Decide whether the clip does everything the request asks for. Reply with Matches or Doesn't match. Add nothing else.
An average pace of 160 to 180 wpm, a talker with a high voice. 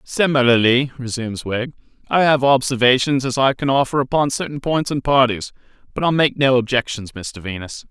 Doesn't match